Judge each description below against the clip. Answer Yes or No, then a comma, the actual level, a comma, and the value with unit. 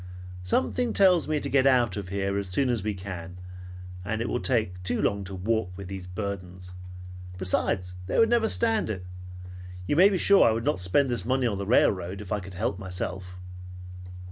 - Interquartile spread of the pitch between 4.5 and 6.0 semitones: Yes, wide, 5.6 semitones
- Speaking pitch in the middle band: No, low, 100 Hz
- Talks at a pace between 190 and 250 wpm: Yes, average, 200 wpm